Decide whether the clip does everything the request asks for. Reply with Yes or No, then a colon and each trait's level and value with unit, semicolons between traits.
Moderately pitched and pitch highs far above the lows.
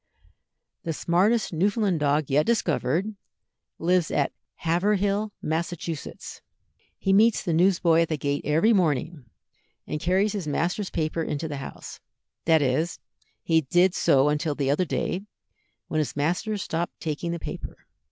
No: medium, 165 Hz; average, 3.9 semitones